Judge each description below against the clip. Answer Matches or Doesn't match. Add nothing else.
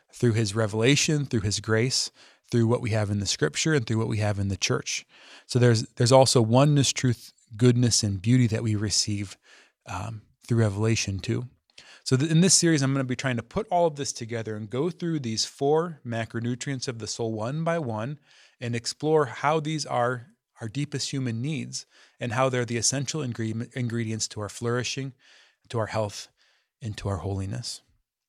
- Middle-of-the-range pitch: Doesn't match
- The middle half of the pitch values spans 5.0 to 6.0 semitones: Doesn't match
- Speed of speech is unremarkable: Matches